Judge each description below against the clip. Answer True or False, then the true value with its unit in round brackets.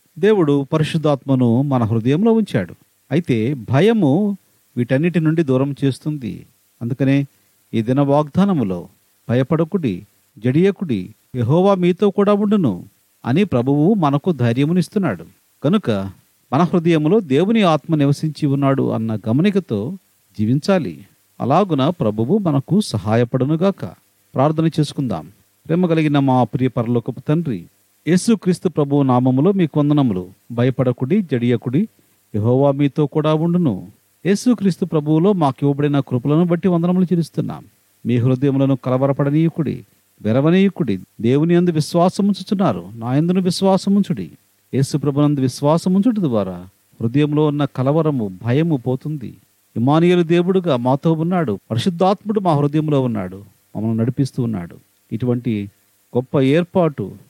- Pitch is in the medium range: True (145 Hz)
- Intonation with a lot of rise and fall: True (6.1 semitones)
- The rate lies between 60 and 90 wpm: False (100 wpm)